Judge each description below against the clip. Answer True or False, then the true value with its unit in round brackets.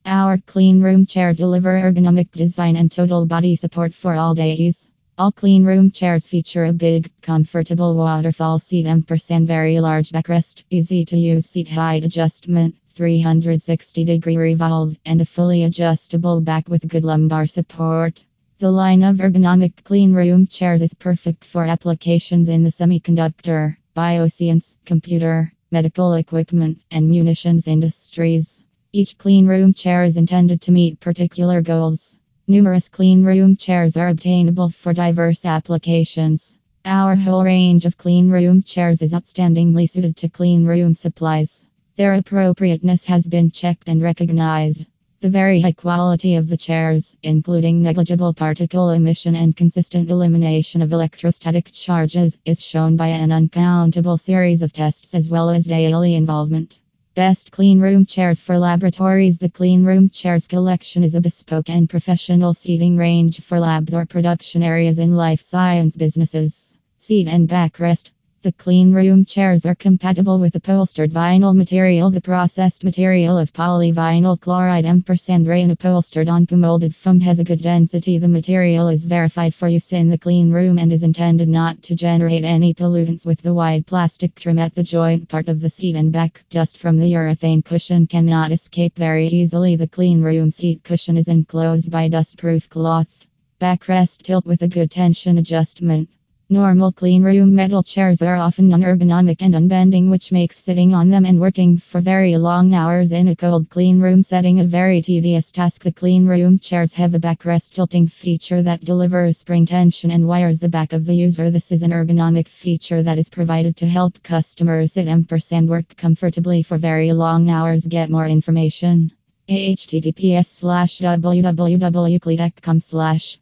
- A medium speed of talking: True (160 wpm)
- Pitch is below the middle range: False (170 Hz)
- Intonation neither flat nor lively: False (1.5 semitones)